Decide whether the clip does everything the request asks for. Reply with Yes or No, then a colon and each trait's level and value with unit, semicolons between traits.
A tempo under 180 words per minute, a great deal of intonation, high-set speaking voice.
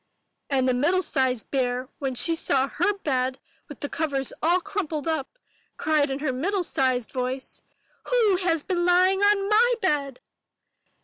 Yes: average, 160 wpm; wide, 5.8 semitones; very high, 300 Hz